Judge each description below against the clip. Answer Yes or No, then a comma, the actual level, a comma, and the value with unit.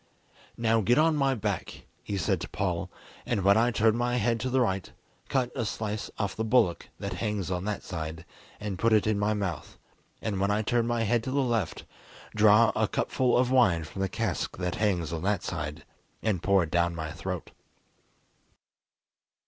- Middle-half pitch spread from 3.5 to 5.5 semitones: Yes, average, 4.2 semitones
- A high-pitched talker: No, low, 105 Hz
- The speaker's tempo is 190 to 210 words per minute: Yes, average, 195 wpm